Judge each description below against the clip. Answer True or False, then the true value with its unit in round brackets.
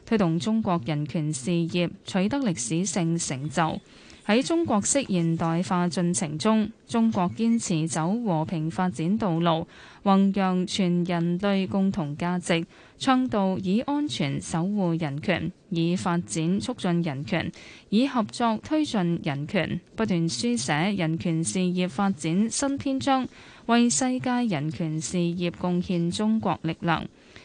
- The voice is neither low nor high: True (180 Hz)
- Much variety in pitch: False (4.3 semitones)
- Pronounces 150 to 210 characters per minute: True (205 characters per minute)